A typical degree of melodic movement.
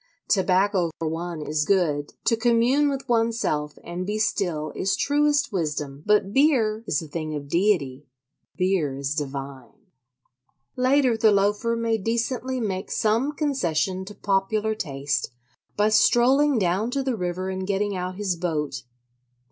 No: wide, 6.5 semitones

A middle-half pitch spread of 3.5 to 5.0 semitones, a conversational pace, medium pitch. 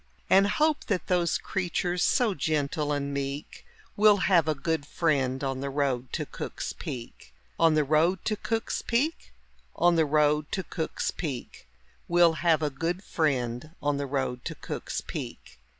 Yes: average, 4.1 semitones; average, 165 wpm; medium, 155 Hz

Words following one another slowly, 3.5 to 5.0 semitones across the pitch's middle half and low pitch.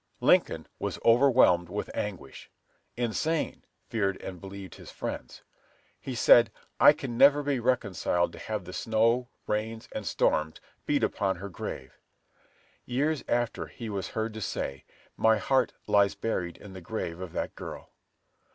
No: average, 150 wpm; average, 4.2 semitones; low, 110 Hz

